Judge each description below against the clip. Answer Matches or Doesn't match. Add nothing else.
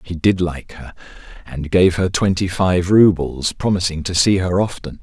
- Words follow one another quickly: Doesn't match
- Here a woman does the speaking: Doesn't match